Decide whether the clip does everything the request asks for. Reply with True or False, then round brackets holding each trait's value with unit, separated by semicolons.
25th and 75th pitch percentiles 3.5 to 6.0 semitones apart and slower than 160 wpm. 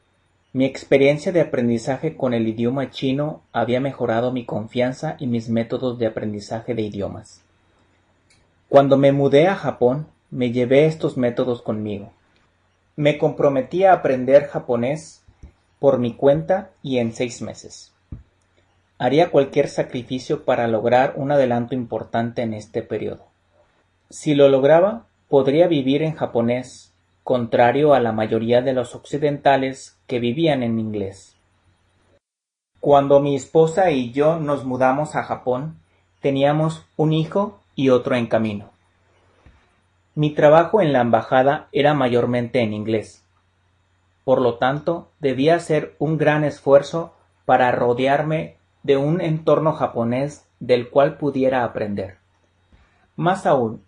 True (4.9 semitones; 130 wpm)